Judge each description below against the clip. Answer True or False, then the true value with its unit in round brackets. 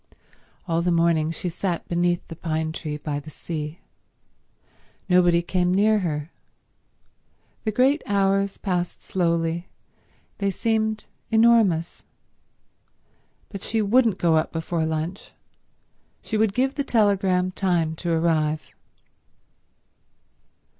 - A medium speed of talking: False (115 wpm)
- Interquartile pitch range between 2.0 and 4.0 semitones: True (3.6 semitones)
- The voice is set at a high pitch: False (175 Hz)